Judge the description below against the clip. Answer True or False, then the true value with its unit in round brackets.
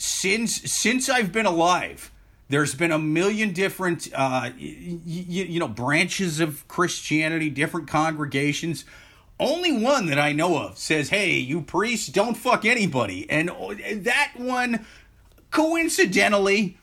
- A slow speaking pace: True (130 wpm)